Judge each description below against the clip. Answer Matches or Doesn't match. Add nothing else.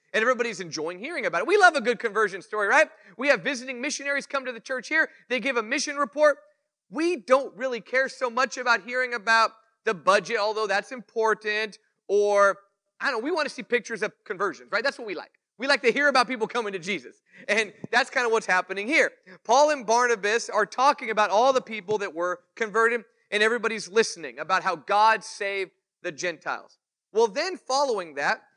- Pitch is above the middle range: Matches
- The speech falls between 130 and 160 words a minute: Doesn't match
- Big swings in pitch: Doesn't match